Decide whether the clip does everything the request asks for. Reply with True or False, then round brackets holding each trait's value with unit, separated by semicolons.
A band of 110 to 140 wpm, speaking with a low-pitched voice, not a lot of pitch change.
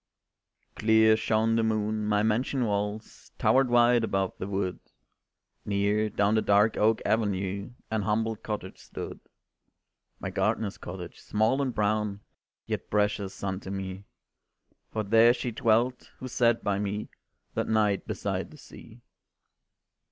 True (135 wpm; 110 Hz; 1.9 semitones)